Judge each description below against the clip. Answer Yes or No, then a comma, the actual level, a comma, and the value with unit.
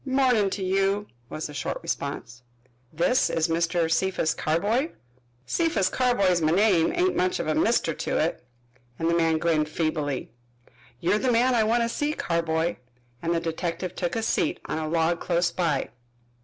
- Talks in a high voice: No, medium, 170 Hz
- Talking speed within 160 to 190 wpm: Yes, average, 170 wpm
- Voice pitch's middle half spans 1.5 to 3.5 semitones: No, average, 4.9 semitones